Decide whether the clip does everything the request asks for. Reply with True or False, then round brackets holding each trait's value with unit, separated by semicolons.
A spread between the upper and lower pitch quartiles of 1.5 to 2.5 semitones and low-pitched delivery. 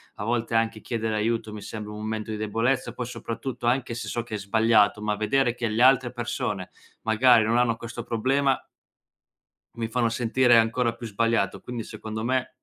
True (1.9 semitones; 115 Hz)